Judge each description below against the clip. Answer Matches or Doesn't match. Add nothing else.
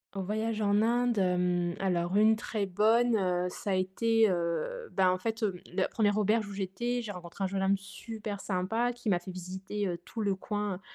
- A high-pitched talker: Matches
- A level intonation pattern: Doesn't match